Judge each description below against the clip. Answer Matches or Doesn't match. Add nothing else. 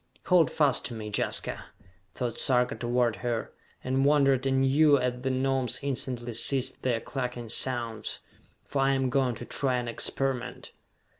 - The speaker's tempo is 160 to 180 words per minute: Doesn't match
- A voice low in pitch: Matches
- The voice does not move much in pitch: Matches